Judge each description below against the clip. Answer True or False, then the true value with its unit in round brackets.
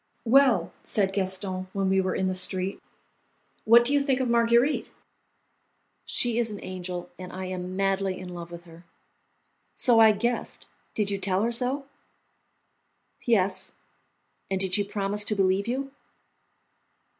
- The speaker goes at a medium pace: True (150 wpm)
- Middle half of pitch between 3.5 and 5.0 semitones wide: True (4.0 semitones)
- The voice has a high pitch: True (195 Hz)